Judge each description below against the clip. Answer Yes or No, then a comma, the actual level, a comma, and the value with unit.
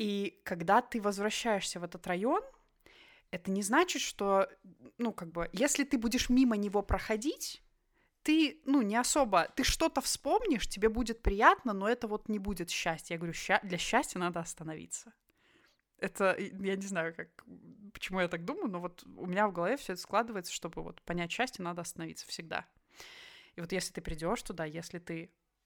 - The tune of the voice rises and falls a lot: Yes, wide, 5.8 semitones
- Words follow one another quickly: Yes, fast, 175 wpm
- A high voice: Yes, high, 205 Hz